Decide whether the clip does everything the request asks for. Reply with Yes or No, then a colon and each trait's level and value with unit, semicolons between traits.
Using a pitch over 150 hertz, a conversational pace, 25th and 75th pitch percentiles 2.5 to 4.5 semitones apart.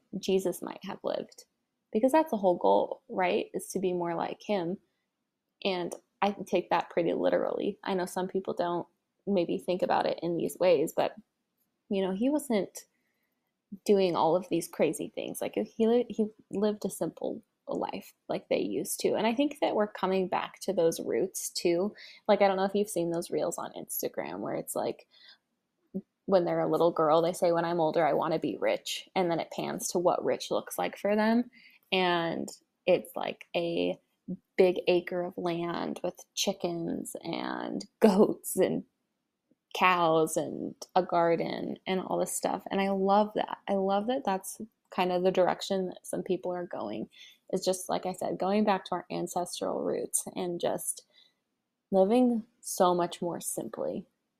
Yes: high, 190 Hz; average, 180 wpm; average, 3.4 semitones